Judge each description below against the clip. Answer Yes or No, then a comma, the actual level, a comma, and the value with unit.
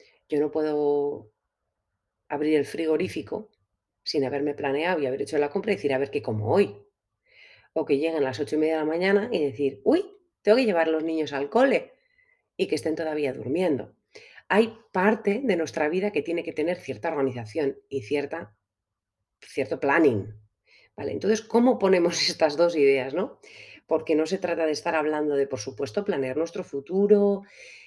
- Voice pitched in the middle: Yes, medium, 155 Hz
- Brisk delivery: No, average, 180 wpm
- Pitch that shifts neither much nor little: No, wide, 6.2 semitones